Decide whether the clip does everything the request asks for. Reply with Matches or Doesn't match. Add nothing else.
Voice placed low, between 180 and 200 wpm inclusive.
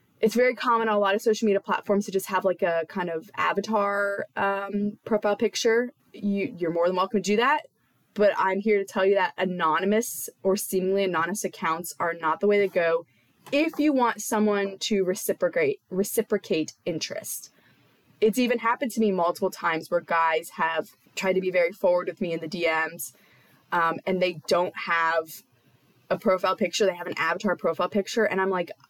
Doesn't match